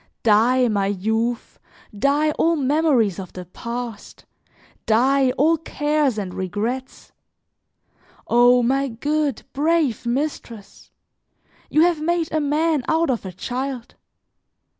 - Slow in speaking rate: Yes, slow, 115 wpm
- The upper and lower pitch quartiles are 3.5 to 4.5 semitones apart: No, average, 5.0 semitones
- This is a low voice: No, very high, 255 Hz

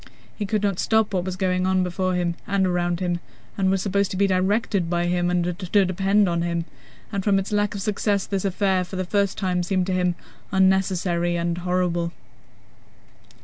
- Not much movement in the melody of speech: Yes, narrow, 1.9 semitones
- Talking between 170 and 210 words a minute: Yes, average, 195 wpm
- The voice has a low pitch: No, medium, 185 Hz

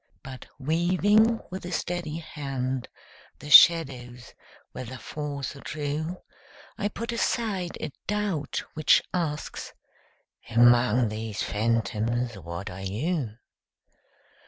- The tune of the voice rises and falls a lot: Yes, wide, 6.4 semitones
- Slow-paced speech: Yes, slow, 105 wpm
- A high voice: No, medium, 140 Hz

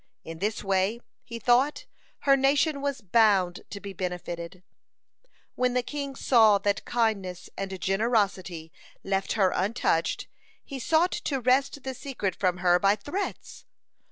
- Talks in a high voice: Yes, high, 210 Hz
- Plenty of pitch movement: Yes, wide, 5.8 semitones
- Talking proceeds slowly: No, average, 145 wpm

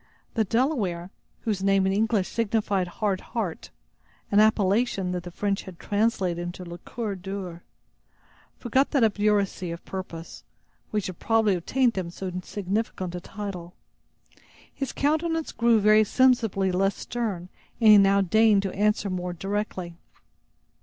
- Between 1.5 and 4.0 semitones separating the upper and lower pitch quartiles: Yes, average, 3.3 semitones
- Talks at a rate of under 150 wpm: Yes, average, 140 wpm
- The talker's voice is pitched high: Yes, high, 200 Hz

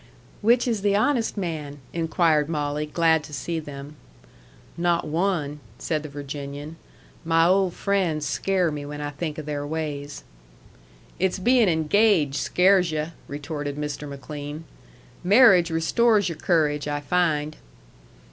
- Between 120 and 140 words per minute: Yes, slow, 135 wpm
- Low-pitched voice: No, medium, 160 Hz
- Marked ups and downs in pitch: No, average, 3.5 semitones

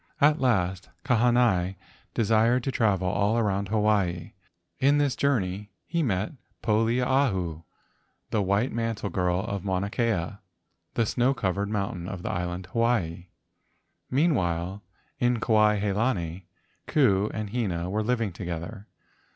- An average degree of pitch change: Yes, average, 4.3 semitones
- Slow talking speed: Yes, slow, 130 wpm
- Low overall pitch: Yes, low, 105 Hz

